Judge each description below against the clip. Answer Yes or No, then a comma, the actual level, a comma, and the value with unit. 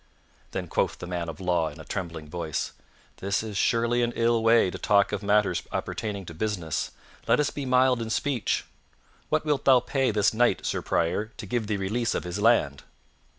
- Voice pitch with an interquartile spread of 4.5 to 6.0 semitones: Yes, average, 5.0 semitones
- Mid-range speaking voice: No, low, 105 Hz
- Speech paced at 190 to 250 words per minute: Yes, average, 195 wpm